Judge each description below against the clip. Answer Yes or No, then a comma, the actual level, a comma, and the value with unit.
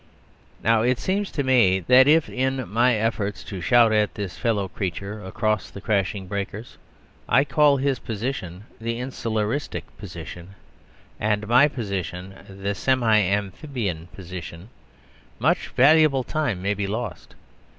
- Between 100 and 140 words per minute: Yes, slow, 135 wpm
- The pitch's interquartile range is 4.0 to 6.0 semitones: Yes, average, 4.7 semitones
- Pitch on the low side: Yes, low, 110 Hz